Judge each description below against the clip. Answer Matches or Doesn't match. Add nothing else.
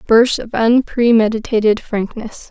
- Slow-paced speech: Matches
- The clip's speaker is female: Matches